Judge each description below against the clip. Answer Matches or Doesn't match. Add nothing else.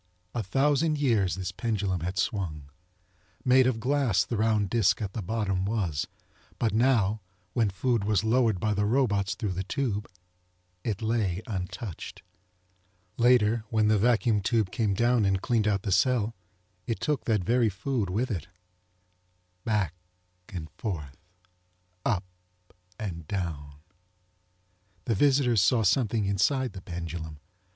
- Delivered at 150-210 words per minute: Doesn't match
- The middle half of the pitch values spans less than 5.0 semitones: Matches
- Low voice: Matches